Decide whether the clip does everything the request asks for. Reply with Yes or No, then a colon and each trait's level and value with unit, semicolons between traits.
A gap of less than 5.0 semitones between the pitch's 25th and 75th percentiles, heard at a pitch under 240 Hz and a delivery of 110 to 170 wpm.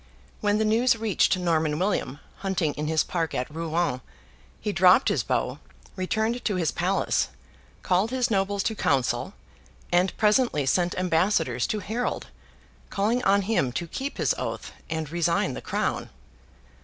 Yes: average, 4.6 semitones; medium, 185 Hz; average, 150 wpm